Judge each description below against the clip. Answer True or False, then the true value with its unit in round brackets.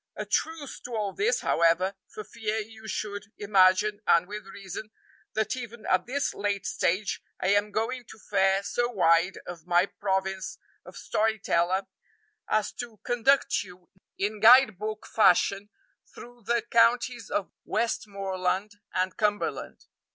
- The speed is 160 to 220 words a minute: False (145 wpm)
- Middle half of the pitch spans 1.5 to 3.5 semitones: True (2.7 semitones)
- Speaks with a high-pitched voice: True (210 Hz)